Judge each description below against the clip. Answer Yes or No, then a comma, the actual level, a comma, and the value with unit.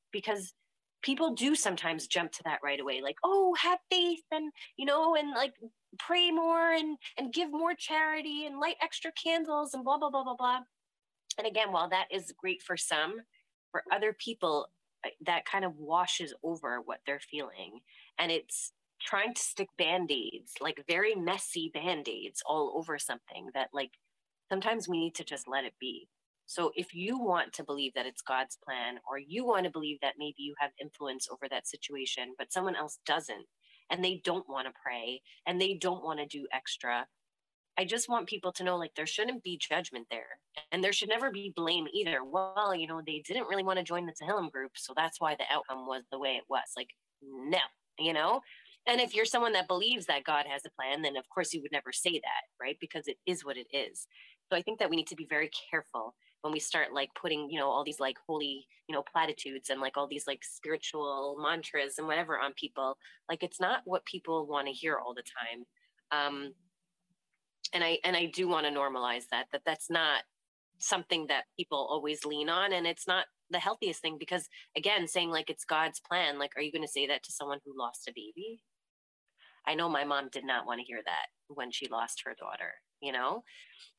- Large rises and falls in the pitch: Yes, wide, 7.1 semitones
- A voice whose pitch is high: No, medium, 170 Hz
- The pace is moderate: No, fast, 215 wpm